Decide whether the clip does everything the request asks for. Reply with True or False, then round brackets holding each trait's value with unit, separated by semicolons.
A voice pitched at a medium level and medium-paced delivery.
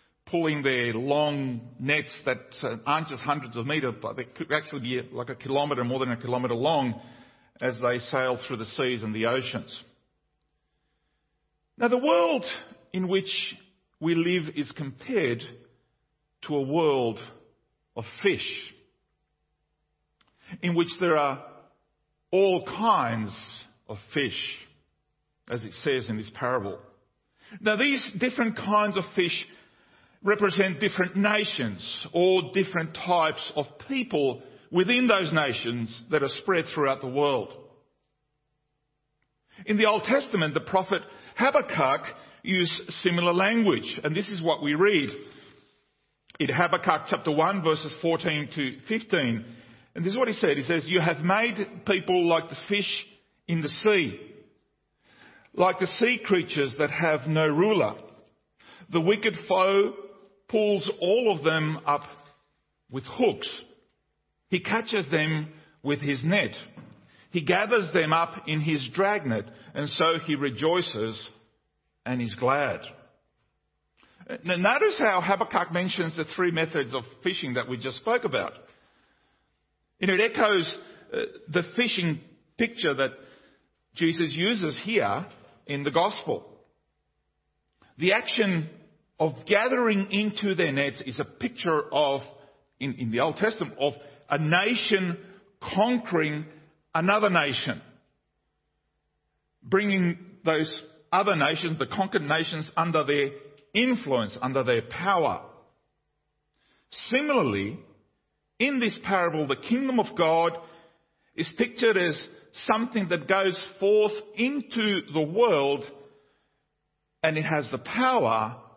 False (165 Hz; 125 wpm)